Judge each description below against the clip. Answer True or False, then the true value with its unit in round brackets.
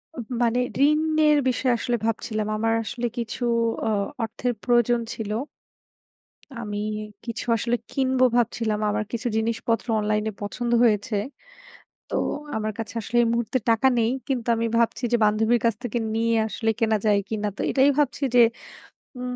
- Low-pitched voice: False (230 Hz)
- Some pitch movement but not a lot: False (1.9 semitones)